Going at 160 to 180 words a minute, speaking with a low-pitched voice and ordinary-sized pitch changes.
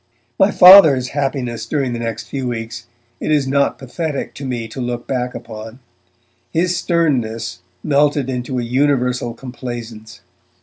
No: average, 140 wpm; low, 125 Hz; average, 3.1 semitones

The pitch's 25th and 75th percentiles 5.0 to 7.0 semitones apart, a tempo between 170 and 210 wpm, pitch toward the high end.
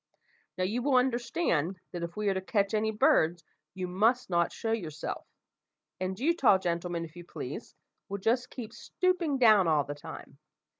Yes: wide, 5.6 semitones; average, 180 wpm; high, 200 Hz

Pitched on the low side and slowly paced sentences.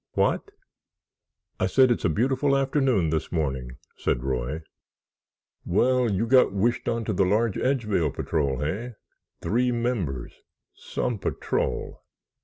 Yes: low, 105 Hz; slow, 120 wpm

